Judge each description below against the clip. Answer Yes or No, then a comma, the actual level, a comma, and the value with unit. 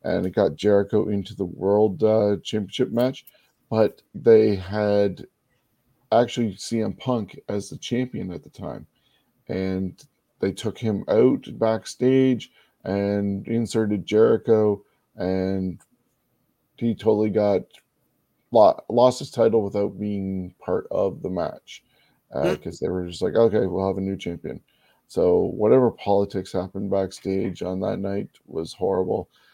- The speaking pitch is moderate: No, low, 100 Hz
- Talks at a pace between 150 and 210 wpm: No, slow, 135 wpm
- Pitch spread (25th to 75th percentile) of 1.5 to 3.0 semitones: Yes, narrow, 2.6 semitones